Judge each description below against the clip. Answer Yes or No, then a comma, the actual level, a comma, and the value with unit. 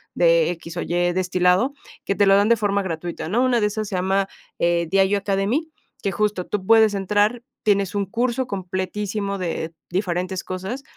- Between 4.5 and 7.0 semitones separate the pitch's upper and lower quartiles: No, narrow, 2.5 semitones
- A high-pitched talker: Yes, high, 195 Hz